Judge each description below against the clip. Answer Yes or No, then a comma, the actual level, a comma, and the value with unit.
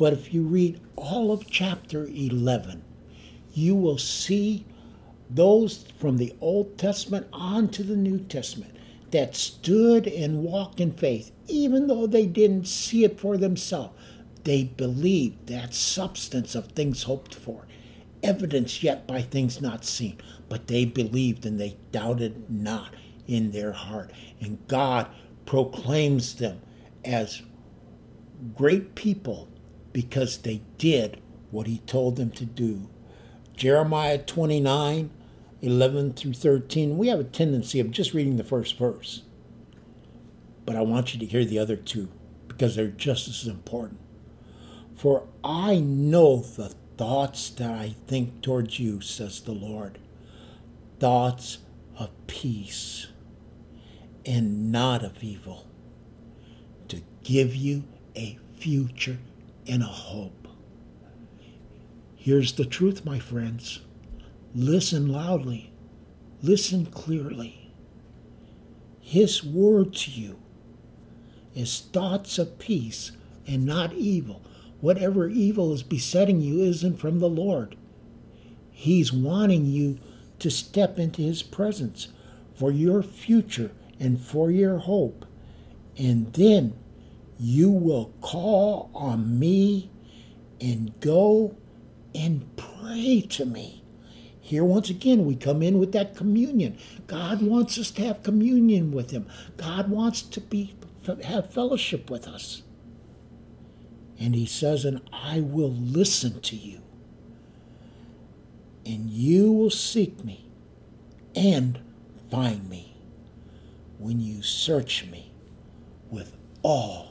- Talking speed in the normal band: No, slow, 120 wpm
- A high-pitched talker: No, low, 135 Hz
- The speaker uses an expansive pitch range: Yes, wide, 8.0 semitones